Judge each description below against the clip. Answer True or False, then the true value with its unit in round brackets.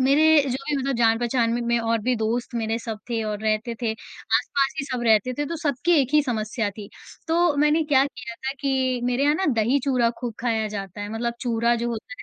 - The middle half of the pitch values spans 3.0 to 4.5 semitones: True (3.4 semitones)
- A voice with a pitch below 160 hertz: False (240 Hz)